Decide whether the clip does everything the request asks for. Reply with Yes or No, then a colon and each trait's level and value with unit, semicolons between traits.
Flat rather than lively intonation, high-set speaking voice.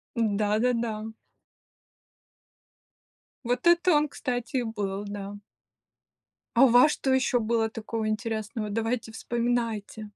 Yes: narrow, 2.3 semitones; high, 225 Hz